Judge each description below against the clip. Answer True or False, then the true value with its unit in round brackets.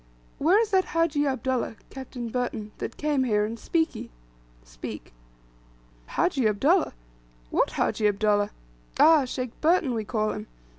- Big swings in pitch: True (6.3 semitones)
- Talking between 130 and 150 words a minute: True (135 wpm)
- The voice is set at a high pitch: True (255 Hz)